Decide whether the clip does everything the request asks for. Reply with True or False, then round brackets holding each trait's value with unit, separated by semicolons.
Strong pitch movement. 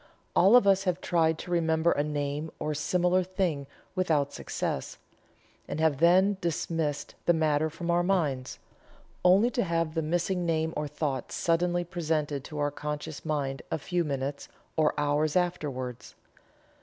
False (3.1 semitones)